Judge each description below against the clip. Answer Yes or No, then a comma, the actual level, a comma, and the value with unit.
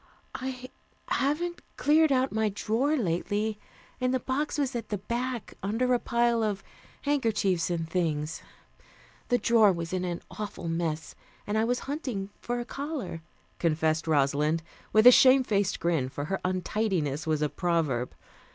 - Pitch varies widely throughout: Yes, wide, 7.1 semitones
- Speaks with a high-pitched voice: Yes, high, 210 Hz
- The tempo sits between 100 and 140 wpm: No, average, 155 wpm